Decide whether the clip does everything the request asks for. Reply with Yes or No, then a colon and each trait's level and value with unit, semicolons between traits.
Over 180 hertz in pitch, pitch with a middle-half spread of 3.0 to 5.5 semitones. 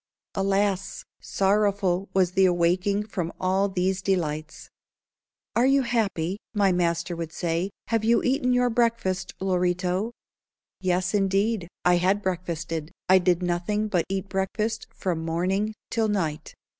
No: high, 190 Hz; narrow, 2.6 semitones